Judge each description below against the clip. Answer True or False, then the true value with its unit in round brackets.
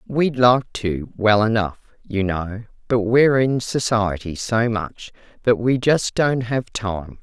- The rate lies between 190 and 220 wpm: False (160 wpm)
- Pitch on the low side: True (115 Hz)